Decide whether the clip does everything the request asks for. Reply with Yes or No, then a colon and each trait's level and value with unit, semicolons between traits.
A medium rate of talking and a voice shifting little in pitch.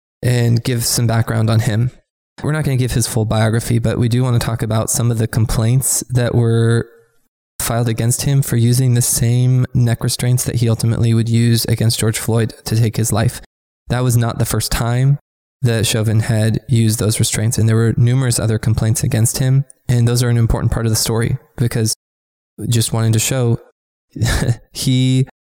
Yes: average, 195 wpm; narrow, 1.7 semitones